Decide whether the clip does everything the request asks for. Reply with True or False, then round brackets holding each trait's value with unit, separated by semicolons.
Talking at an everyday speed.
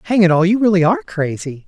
False (250 wpm)